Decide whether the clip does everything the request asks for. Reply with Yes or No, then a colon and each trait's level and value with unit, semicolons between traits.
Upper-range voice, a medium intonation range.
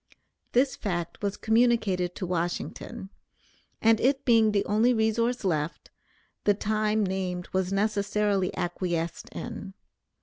Yes: high, 205 Hz; average, 3.4 semitones